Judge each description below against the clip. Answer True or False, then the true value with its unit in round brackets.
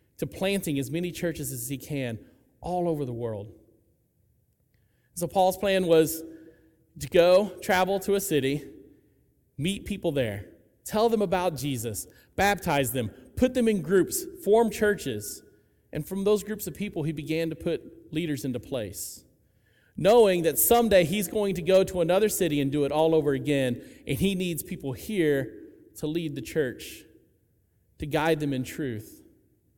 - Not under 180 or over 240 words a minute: False (160 wpm)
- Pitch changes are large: True (5.9 semitones)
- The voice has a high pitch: False (160 Hz)